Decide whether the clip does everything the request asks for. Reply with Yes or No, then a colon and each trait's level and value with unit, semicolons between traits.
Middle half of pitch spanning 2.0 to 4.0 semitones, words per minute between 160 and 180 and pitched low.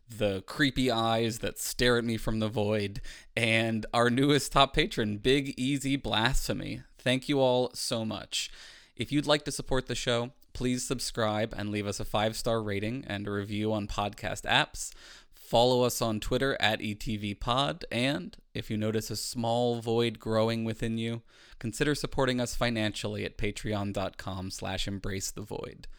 Yes: average, 2.9 semitones; average, 165 wpm; low, 115 Hz